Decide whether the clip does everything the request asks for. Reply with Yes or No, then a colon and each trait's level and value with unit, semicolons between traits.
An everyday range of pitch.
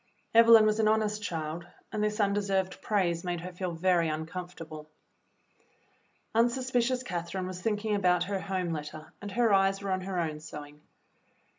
Yes: average, 3.8 semitones